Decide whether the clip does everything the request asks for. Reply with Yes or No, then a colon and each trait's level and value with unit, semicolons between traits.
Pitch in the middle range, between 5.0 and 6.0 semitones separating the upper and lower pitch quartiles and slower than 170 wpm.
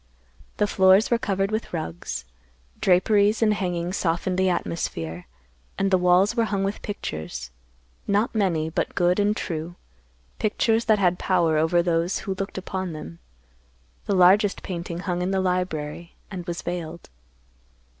No: medium, 180 Hz; average, 2.8 semitones; average, 150 wpm